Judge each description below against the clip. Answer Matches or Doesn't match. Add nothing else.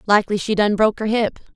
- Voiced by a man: Doesn't match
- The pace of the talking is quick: Matches